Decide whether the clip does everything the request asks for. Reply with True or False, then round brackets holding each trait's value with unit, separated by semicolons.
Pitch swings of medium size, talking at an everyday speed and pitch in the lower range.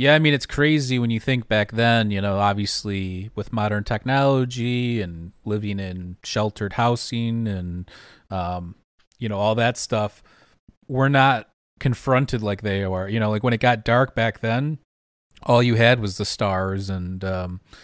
True (3.8 semitones; 170 wpm; 110 Hz)